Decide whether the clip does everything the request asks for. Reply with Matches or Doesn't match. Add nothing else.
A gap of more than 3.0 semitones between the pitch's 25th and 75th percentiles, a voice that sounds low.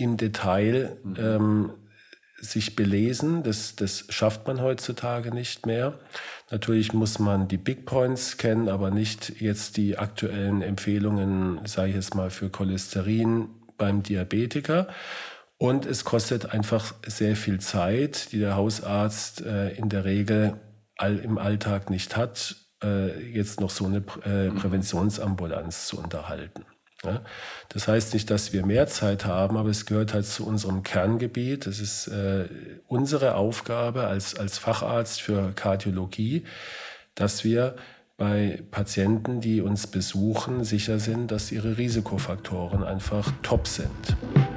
Doesn't match